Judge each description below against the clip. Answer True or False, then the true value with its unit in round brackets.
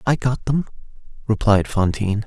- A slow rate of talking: True (130 wpm)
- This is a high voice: False (115 Hz)